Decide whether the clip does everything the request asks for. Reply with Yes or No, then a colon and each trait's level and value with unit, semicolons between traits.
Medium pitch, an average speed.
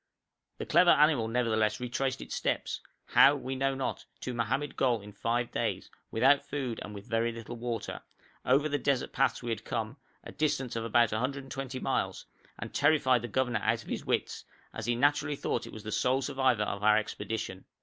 No: low, 125 Hz; average, 190 wpm